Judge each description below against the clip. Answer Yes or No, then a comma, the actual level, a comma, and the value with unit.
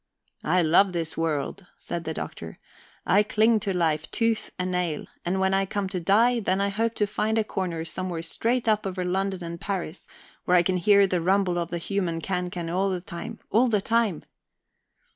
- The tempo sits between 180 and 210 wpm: Yes, average, 200 wpm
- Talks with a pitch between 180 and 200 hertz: Yes, medium, 185 Hz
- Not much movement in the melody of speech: No, average, 3.0 semitones